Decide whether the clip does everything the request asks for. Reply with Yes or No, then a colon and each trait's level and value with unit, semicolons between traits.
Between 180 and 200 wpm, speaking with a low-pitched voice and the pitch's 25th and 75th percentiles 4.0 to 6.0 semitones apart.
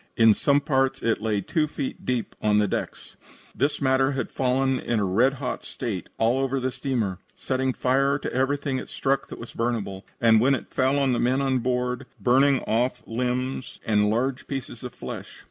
No: average, 195 wpm; low, 130 Hz; average, 2.7 semitones